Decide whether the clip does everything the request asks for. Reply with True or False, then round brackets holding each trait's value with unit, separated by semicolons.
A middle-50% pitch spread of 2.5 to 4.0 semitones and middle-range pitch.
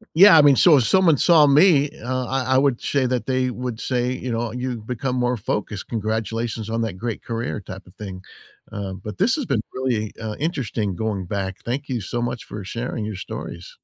False (3.6 semitones; 120 Hz)